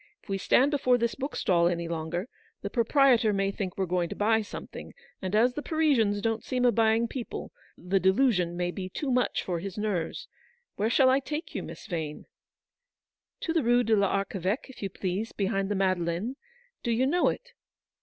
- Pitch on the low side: No, high, 210 Hz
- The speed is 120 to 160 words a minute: No, average, 195 wpm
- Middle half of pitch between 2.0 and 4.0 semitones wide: No, average, 5.1 semitones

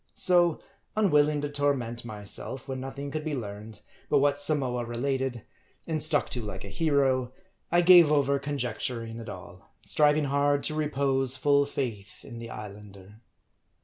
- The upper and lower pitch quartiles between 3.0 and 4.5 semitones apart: Yes, average, 4.0 semitones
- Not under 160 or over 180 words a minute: No, average, 150 wpm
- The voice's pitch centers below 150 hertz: Yes, low, 135 Hz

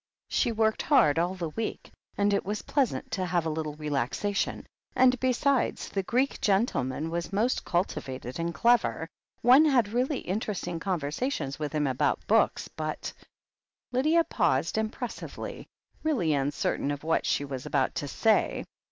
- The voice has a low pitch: No, medium, 185 Hz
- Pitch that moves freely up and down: Yes, wide, 7.9 semitones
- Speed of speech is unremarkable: Yes, average, 155 wpm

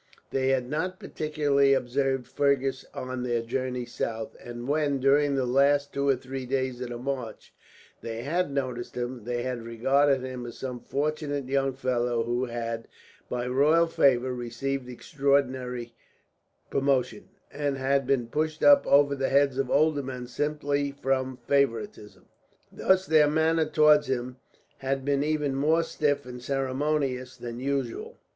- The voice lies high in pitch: No, low, 135 Hz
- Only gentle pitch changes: Yes, narrow, 2.3 semitones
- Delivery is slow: No, average, 150 wpm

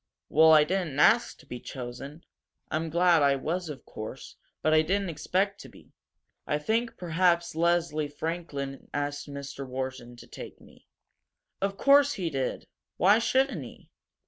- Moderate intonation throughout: Yes, average, 4.3 semitones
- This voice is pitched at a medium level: Yes, medium, 160 Hz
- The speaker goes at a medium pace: Yes, average, 155 wpm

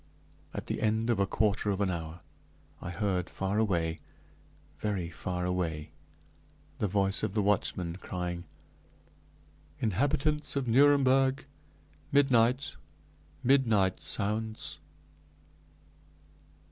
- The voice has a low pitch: Yes, low, 105 Hz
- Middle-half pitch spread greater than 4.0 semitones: Yes, average, 5.0 semitones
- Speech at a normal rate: No, slow, 100 wpm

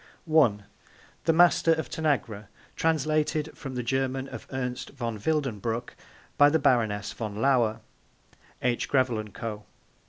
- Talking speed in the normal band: No, slow, 130 wpm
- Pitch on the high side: No, low, 130 Hz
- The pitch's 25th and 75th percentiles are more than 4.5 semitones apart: Yes, average, 5.1 semitones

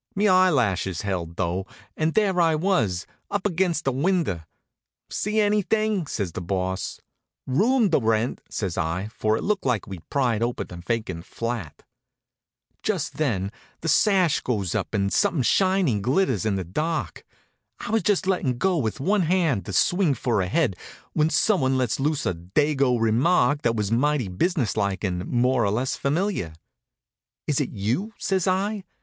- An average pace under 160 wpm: No, average, 165 wpm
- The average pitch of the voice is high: No, low, 130 Hz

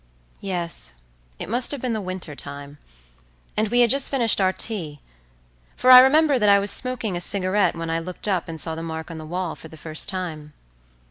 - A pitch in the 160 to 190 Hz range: Yes, medium, 185 Hz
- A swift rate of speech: Yes, fast, 210 wpm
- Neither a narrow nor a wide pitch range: No, wide, 5.8 semitones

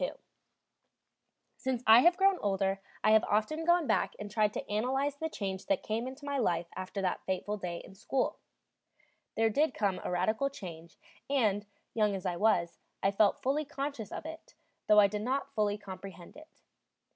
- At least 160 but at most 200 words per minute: Yes, average, 180 wpm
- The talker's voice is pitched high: Yes, high, 215 Hz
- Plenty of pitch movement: Yes, wide, 5.9 semitones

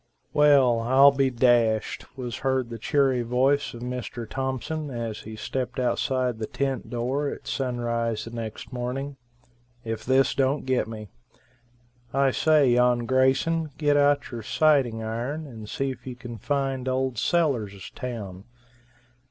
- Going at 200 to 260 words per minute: No, average, 145 wpm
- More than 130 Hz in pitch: No, low, 125 Hz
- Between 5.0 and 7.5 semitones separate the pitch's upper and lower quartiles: No, average, 2.7 semitones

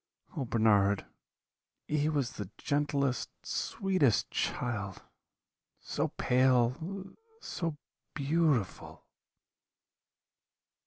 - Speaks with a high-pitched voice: No, low, 135 Hz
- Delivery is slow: Yes, slow, 65 wpm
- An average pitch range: Yes, average, 4.8 semitones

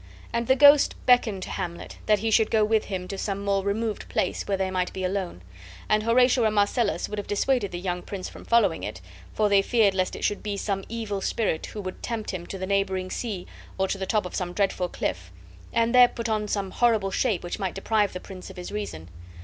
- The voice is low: No, high, 200 Hz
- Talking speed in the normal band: No, fast, 235 wpm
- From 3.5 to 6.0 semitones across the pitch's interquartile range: No, average, 2.9 semitones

